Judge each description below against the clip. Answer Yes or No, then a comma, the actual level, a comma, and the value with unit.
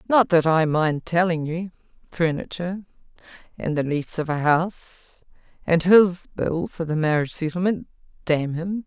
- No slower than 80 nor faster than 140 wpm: Yes, slow, 135 wpm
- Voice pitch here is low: No, medium, 170 Hz